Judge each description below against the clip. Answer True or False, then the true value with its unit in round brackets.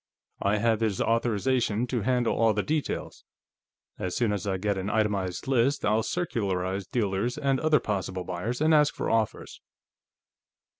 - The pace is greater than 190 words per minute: False (155 wpm)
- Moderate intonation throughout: True (3.9 semitones)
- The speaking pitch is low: True (110 Hz)